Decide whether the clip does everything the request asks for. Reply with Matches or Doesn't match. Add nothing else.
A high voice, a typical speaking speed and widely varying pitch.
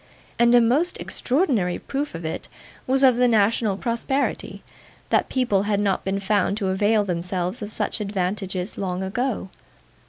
Doesn't match